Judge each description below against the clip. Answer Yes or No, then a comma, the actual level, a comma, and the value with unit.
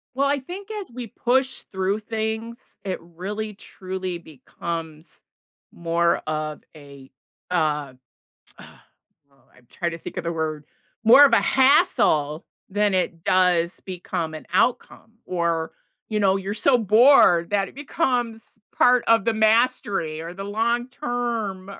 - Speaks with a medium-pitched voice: No, high, 195 Hz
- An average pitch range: No, wide, 5.7 semitones